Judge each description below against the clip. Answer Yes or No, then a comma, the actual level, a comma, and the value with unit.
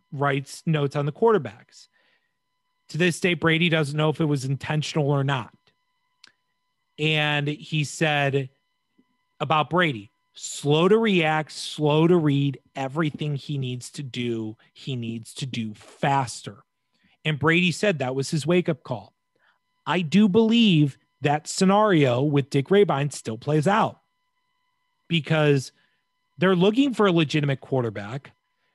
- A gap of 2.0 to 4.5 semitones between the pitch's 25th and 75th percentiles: No, wide, 5.6 semitones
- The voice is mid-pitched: Yes, medium, 155 Hz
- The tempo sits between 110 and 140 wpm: Yes, slow, 135 wpm